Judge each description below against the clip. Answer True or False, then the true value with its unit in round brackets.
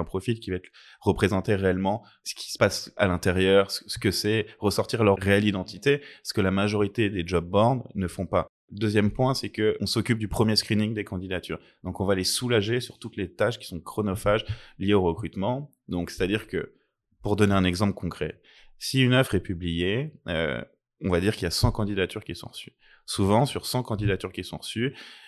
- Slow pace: False (215 wpm)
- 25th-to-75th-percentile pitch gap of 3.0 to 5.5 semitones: False (2.5 semitones)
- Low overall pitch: True (100 Hz)